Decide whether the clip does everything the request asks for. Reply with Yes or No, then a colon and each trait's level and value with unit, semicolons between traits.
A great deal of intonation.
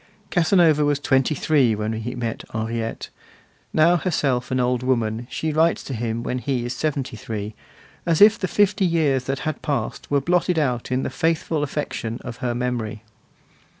No: average, 4.8 semitones